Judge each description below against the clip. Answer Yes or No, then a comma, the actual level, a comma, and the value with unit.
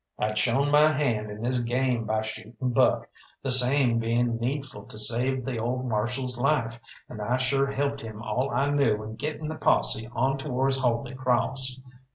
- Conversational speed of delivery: Yes, average, 180 wpm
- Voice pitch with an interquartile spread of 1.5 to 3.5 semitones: Yes, average, 2.9 semitones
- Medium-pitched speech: No, low, 125 Hz